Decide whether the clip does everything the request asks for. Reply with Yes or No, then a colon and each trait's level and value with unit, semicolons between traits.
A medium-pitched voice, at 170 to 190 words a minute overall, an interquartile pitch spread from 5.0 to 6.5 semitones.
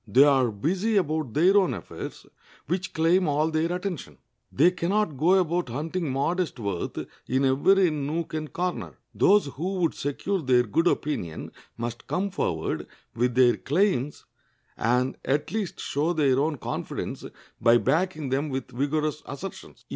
No: medium, 155 Hz; average, 155 wpm; average, 5.3 semitones